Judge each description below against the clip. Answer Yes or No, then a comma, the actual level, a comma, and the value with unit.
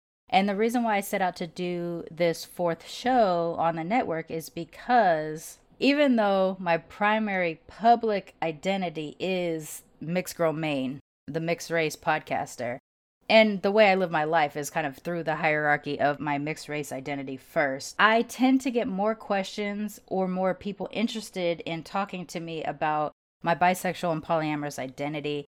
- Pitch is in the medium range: Yes, medium, 170 Hz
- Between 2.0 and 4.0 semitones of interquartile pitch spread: No, average, 4.5 semitones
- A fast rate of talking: No, average, 165 wpm